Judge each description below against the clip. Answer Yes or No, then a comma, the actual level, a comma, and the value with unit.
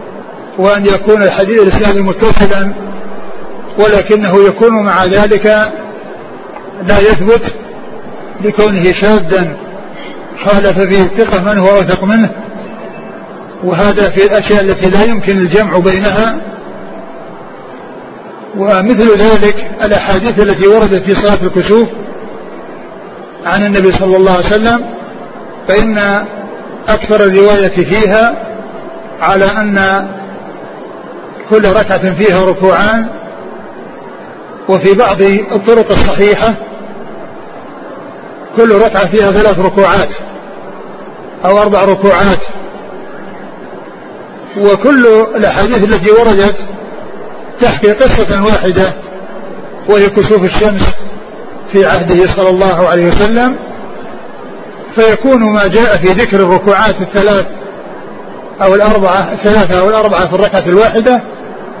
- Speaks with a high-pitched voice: Yes, high, 205 Hz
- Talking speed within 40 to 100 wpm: Yes, average, 90 wpm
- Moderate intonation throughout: No, narrow, 1.7 semitones